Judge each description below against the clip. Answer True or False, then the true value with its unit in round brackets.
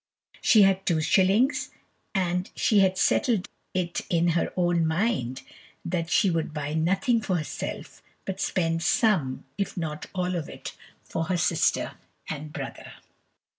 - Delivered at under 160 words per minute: True (145 wpm)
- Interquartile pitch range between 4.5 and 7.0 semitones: False (3.0 semitones)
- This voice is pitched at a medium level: True (175 Hz)